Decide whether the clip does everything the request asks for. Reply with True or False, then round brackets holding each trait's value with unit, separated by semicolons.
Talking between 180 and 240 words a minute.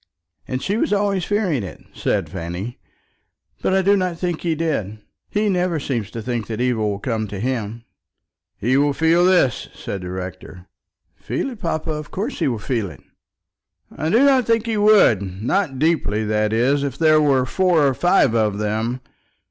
True (185 wpm)